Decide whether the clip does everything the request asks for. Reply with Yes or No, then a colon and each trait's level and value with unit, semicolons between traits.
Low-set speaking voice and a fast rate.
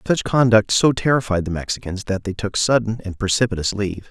No: low, 105 Hz; average, 190 wpm